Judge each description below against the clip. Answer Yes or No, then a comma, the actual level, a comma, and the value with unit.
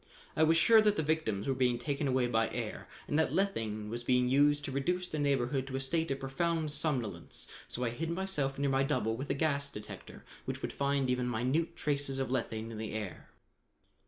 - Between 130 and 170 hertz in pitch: Yes, low, 135 Hz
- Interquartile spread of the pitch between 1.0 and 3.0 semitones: No, average, 3.8 semitones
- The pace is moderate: No, fast, 215 wpm